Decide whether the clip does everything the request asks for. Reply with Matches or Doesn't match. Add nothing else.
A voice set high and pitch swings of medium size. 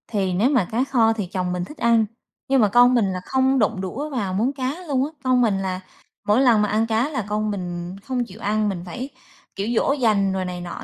Matches